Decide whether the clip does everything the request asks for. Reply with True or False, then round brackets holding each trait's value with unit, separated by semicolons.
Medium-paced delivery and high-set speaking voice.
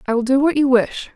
False (310 wpm; 260 Hz)